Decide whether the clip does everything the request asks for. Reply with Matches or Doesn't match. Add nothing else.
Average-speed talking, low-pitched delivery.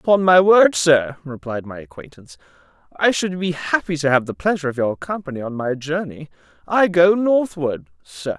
Doesn't match